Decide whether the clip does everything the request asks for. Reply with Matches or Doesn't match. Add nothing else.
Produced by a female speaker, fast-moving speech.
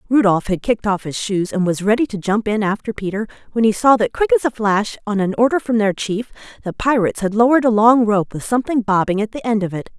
Matches